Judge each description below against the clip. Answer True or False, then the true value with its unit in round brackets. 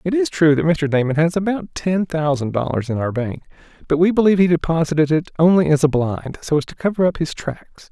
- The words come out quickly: True (235 wpm)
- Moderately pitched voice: True (160 Hz)